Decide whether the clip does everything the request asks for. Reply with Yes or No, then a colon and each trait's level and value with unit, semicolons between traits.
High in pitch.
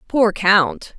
Yes: high, 205 Hz